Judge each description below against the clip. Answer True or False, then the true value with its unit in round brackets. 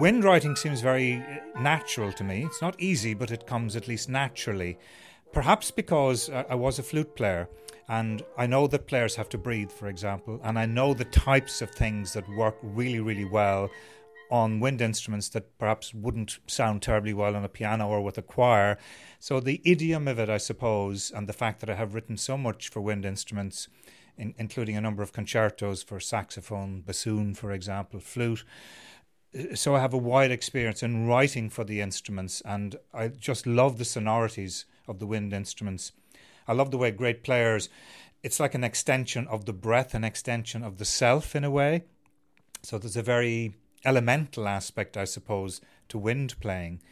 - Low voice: True (115 Hz)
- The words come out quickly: False (185 wpm)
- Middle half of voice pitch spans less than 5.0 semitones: True (3.6 semitones)